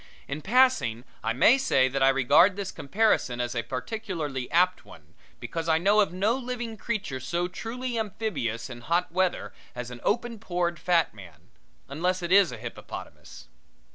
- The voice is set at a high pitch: No, medium, 175 Hz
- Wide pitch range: Yes, wide, 8.5 semitones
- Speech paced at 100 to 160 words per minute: No, average, 170 wpm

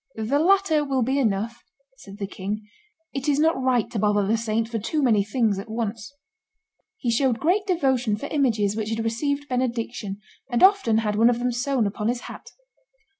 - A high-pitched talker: Yes, high, 235 Hz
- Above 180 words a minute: Yes, average, 190 wpm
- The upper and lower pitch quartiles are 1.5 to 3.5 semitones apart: No, average, 4.2 semitones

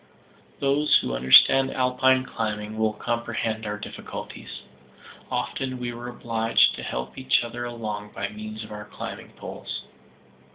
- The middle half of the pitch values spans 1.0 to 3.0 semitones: Yes, average, 2.7 semitones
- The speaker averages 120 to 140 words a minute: Yes, slow, 135 wpm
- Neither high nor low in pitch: No, low, 115 Hz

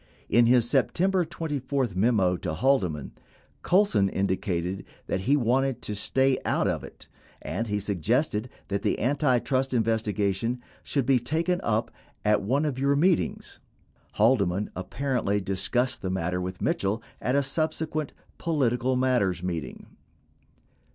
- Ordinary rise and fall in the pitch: No, wide, 5.7 semitones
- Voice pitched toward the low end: Yes, low, 120 Hz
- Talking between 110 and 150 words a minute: Yes, average, 145 wpm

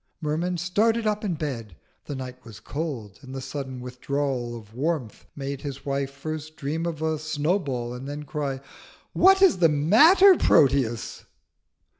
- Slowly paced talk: No, average, 155 wpm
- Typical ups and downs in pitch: Yes, average, 4.2 semitones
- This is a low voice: No, medium, 145 Hz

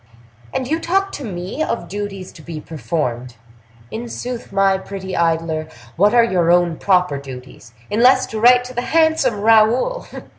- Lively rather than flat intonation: Yes, wide, 6.6 semitones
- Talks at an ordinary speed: Yes, average, 160 wpm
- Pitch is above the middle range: Yes, high, 195 Hz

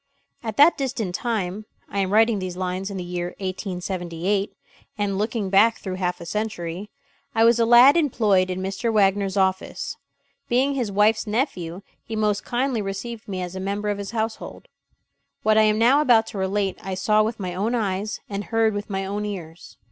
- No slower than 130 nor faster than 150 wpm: No, average, 190 wpm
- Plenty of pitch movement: No, average, 2.9 semitones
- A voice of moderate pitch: No, high, 205 Hz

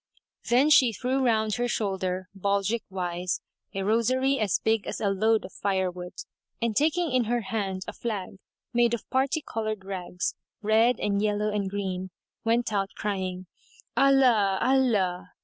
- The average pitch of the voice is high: Yes, high, 215 Hz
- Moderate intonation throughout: Yes, average, 3.9 semitones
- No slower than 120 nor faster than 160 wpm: Yes, average, 150 wpm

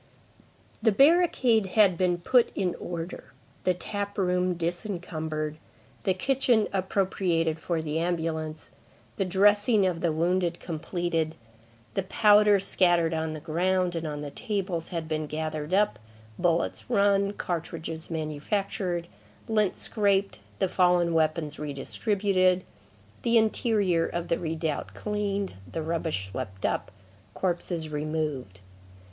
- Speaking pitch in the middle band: Yes, medium, 175 Hz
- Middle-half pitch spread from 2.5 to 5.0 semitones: Yes, average, 3.7 semitones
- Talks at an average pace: No, slow, 125 wpm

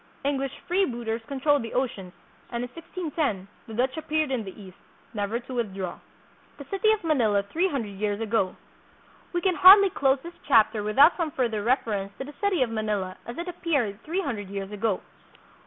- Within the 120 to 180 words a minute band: No, average, 190 wpm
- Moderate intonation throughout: No, wide, 6.8 semitones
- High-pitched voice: Yes, high, 245 Hz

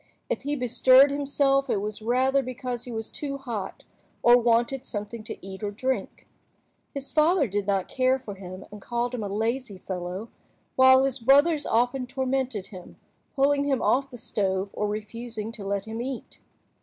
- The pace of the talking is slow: No, average, 175 wpm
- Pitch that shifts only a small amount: No, average, 4.3 semitones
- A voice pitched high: Yes, high, 245 Hz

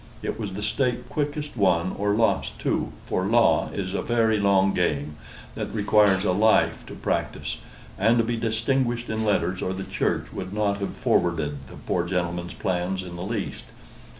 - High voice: No, low, 100 Hz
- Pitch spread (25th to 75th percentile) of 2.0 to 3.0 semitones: No, average, 3.6 semitones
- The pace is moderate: Yes, average, 175 wpm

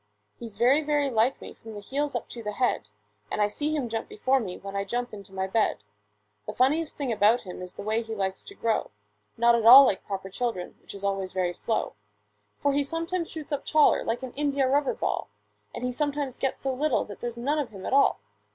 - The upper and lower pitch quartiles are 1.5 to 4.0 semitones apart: No, wide, 5.4 semitones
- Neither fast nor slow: No, fast, 235 wpm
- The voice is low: No, high, 240 Hz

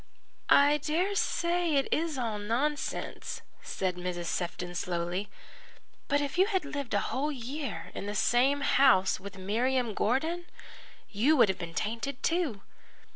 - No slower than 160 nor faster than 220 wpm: No, average, 145 wpm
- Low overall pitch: No, very high, 255 Hz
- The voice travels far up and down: Yes, wide, 6.8 semitones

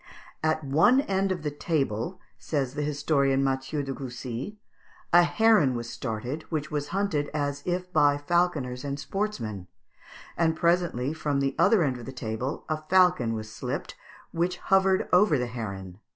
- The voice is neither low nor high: Yes, medium, 145 Hz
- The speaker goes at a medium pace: Yes, average, 160 wpm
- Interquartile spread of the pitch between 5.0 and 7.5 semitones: Yes, average, 5.3 semitones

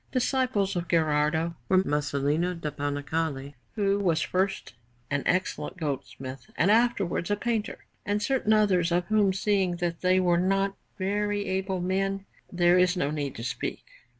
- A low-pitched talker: No, medium, 185 Hz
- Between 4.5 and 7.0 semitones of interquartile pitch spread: No, average, 3.8 semitones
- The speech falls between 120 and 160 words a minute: Yes, average, 150 wpm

